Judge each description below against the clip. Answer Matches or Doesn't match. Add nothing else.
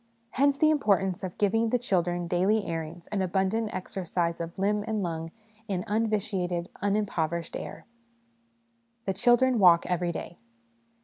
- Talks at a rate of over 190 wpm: Doesn't match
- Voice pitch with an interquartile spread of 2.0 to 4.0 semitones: Matches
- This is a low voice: Doesn't match